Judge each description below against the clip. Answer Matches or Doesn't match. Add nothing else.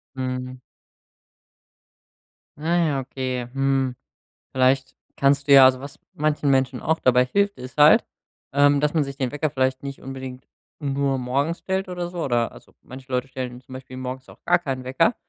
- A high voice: Doesn't match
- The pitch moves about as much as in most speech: Doesn't match